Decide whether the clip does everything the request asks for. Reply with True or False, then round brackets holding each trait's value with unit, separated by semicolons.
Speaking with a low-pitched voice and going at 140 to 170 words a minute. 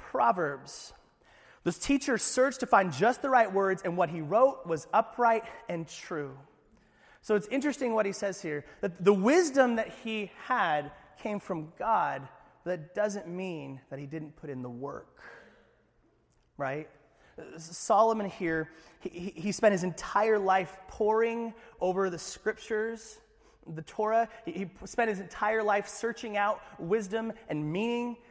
False (205 Hz; 150 wpm)